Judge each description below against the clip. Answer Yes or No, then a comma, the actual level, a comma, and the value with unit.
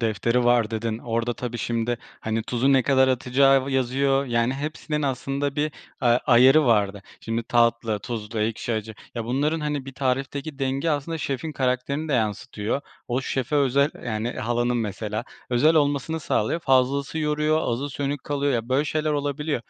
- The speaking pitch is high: No, low, 130 Hz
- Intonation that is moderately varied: Yes, average, 3.4 semitones